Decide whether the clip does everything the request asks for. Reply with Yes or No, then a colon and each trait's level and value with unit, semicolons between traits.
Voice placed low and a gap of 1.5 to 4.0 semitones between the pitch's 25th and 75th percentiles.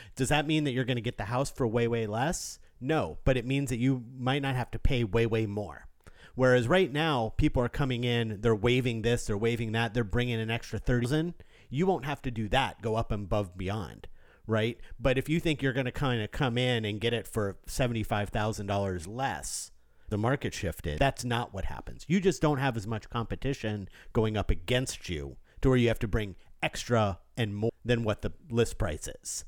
Yes: low, 120 Hz; average, 3.5 semitones